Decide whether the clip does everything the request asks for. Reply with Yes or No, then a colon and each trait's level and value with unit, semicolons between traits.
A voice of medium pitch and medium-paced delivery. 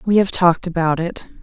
No: medium, 175 Hz; fast, 210 wpm